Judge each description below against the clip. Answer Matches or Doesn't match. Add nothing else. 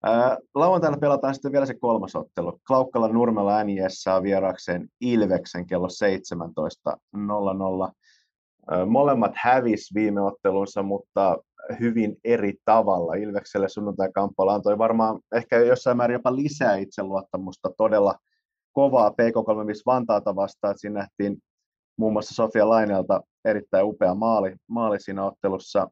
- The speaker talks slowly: Doesn't match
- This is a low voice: Matches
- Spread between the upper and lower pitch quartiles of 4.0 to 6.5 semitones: Doesn't match